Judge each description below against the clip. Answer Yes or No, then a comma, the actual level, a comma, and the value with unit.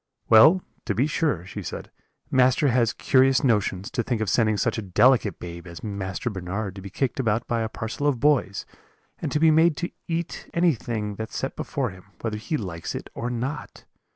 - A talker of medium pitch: No, low, 115 Hz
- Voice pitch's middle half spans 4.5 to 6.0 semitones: Yes, average, 5.0 semitones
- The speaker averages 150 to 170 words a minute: No, average, 200 wpm